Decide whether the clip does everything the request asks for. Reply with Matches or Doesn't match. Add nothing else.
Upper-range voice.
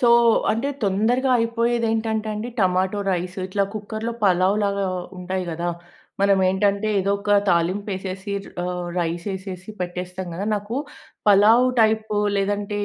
Matches